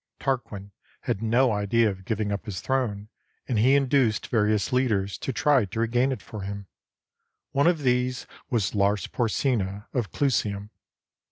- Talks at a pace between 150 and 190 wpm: Yes, average, 155 wpm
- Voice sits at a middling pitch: No, low, 115 Hz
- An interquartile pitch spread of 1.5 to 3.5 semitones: No, average, 3.9 semitones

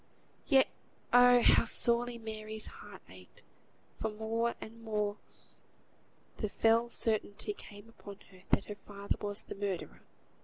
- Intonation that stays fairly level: Yes, narrow, 2.3 semitones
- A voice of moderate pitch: No, high, 220 Hz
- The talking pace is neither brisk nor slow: No, slow, 130 wpm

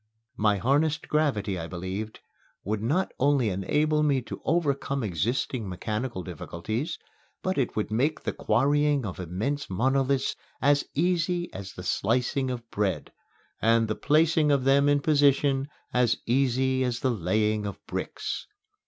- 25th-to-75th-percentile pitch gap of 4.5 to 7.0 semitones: Yes, average, 5.2 semitones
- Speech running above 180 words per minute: No, average, 145 wpm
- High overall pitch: No, low, 130 Hz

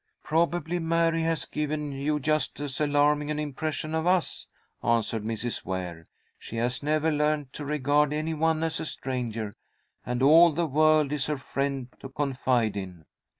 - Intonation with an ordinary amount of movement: Yes, average, 3.3 semitones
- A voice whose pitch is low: No, medium, 150 Hz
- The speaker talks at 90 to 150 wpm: No, average, 160 wpm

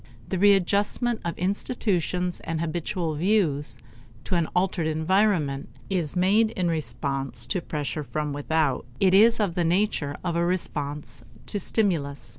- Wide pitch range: No, average, 4.3 semitones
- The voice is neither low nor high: Yes, medium, 170 Hz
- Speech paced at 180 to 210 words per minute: No, average, 140 wpm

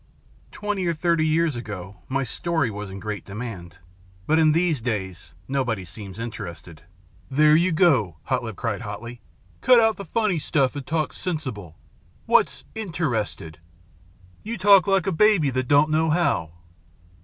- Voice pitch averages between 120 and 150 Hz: Yes, medium, 140 Hz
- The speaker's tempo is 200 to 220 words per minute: No, average, 155 wpm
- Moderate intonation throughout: No, wide, 8.4 semitones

